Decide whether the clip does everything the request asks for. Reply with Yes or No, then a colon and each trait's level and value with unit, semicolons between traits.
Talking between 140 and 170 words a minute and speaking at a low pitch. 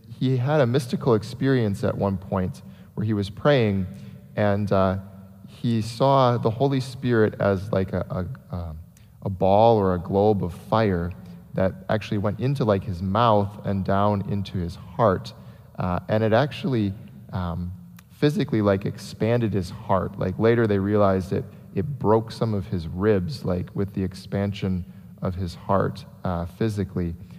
Yes: average, 160 wpm; low, 100 Hz